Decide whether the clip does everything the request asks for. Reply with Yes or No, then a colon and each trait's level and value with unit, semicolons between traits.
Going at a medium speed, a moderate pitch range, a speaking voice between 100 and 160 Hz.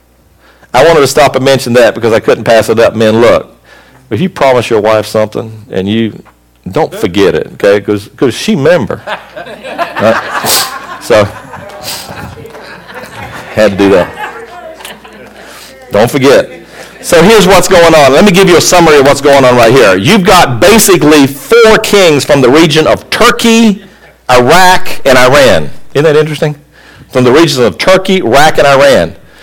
No: average, 160 wpm; wide, 8.9 semitones; medium, 140 Hz